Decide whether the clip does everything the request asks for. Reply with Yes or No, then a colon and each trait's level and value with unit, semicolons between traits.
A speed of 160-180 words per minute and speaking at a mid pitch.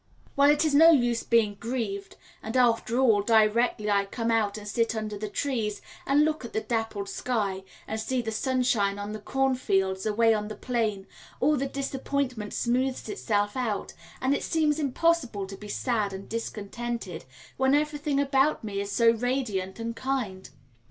No: average, 170 wpm; high, 230 Hz